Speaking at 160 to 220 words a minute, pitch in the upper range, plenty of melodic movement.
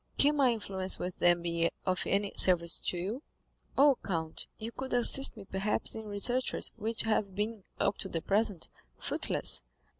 No: average, 170 wpm; high, 205 Hz; average, 3.8 semitones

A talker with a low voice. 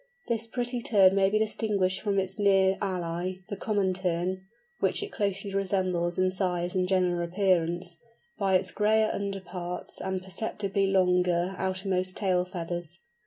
No: high, 190 Hz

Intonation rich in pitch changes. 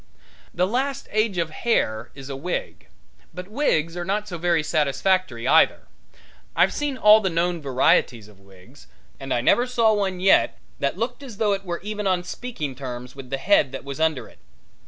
Yes: wide, 7.3 semitones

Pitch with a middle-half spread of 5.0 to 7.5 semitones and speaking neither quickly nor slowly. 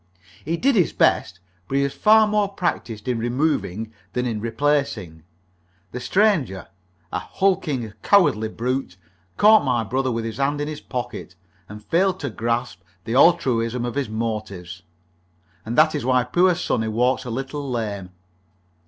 Yes: average, 5.3 semitones; average, 155 wpm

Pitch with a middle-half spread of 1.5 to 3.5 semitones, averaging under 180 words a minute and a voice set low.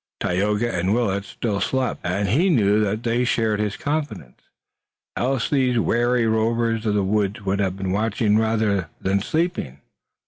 Yes: average, 3.1 semitones; average, 160 wpm; low, 110 Hz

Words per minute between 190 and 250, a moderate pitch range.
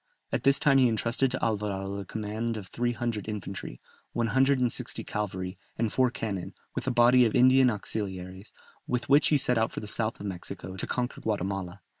Yes: average, 200 wpm; average, 4.0 semitones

